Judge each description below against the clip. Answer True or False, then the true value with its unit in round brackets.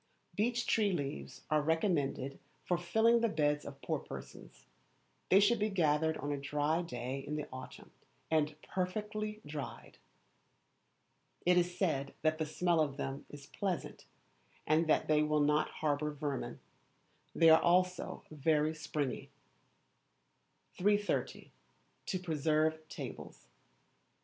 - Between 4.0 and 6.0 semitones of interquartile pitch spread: False (3.6 semitones)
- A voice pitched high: False (155 Hz)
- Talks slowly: True (130 wpm)